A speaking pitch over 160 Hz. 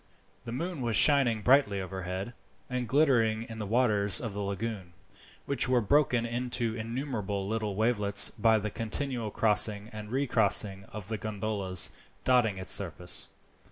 No: low, 110 Hz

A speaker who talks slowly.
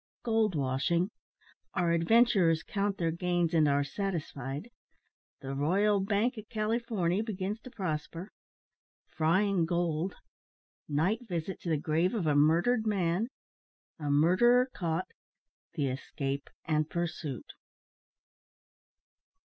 Yes: slow, 110 wpm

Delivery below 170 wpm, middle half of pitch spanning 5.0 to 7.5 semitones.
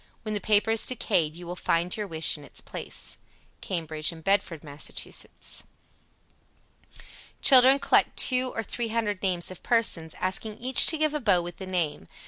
No: average, 175 wpm; average, 5.3 semitones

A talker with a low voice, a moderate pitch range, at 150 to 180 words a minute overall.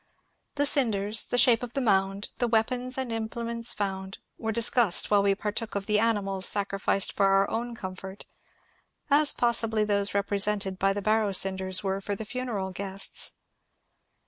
No: high, 210 Hz; average, 3.0 semitones; average, 165 wpm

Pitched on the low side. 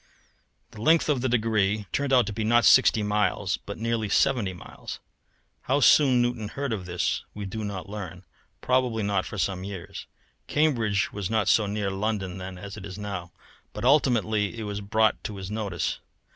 Yes: low, 105 Hz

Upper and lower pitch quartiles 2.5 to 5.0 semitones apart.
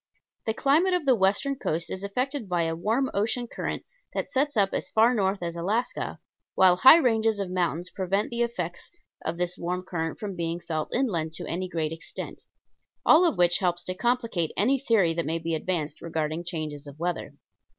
No: wide, 5.5 semitones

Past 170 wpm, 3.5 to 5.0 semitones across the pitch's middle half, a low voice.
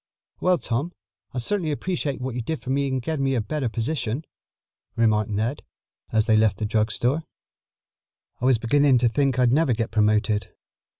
Yes: average, 180 wpm; average, 4.4 semitones; low, 125 Hz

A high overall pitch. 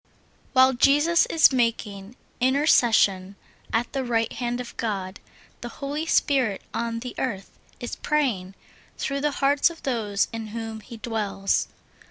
Yes: high, 240 Hz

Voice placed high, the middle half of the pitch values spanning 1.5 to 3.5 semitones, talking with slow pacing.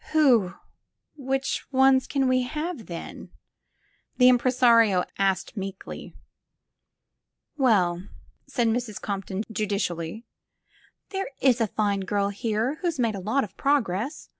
No: high, 230 Hz; average, 5.0 semitones; slow, 125 wpm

